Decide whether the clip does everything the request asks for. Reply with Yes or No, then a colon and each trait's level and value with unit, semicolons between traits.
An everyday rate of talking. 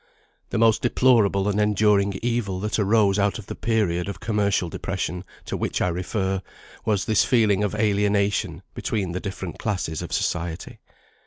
Yes: average, 160 wpm